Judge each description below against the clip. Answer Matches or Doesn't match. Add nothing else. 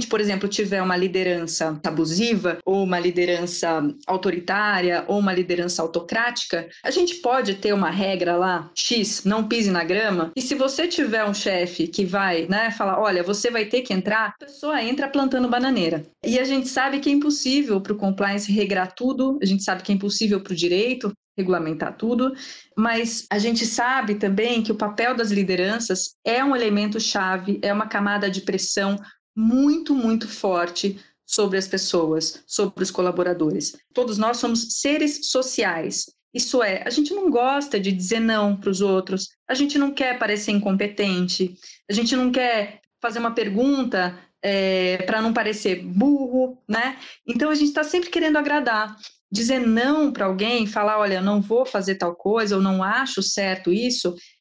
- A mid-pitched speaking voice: Doesn't match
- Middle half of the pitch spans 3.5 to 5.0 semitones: Matches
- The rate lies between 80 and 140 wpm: Doesn't match